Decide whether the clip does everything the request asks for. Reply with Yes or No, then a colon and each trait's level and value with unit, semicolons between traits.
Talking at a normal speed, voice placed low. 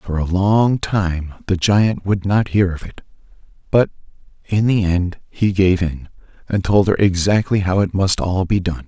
Yes: average, 190 wpm; very low, 95 Hz